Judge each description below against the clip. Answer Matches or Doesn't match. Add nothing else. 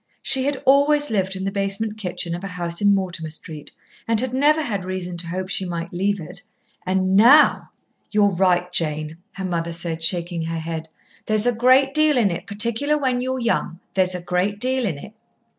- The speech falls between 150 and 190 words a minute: Doesn't match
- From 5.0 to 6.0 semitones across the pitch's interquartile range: Matches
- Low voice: Doesn't match